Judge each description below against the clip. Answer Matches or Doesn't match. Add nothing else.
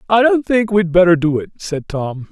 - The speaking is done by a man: Matches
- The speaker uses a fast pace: Matches